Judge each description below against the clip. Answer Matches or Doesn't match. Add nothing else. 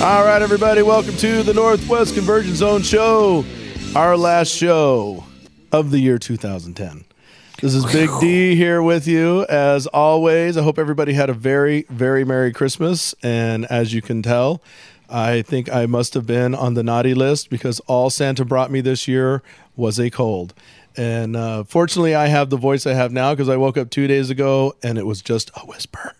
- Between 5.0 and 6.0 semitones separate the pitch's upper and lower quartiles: Matches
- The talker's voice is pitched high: Doesn't match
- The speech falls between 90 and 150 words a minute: Doesn't match